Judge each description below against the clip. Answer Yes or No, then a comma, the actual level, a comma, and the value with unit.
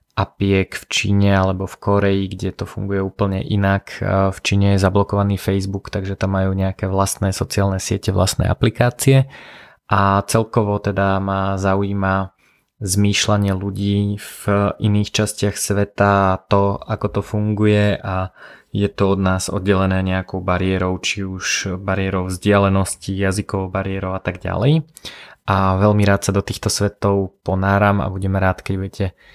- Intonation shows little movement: Yes, narrow, 1.1 semitones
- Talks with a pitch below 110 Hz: Yes, low, 100 Hz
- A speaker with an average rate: Yes, average, 140 wpm